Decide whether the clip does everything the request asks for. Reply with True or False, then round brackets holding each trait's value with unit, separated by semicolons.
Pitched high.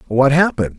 False (150 Hz)